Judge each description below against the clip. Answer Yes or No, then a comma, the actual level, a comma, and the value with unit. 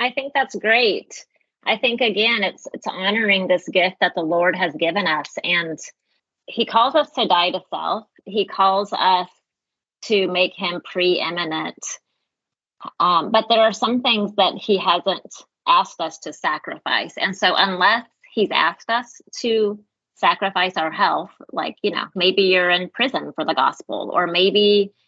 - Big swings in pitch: No, average, 3.7 semitones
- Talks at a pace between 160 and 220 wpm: Yes, average, 165 wpm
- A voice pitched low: No, high, 195 Hz